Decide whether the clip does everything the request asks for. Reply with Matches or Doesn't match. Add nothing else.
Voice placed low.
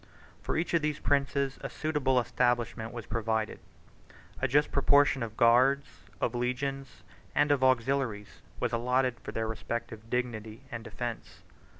Matches